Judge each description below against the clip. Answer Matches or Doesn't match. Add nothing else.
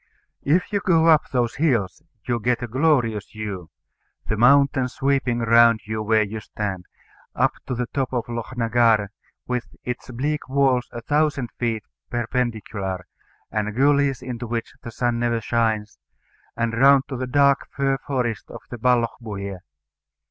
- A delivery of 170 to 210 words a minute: Doesn't match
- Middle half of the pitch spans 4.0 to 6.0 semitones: Doesn't match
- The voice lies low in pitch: Matches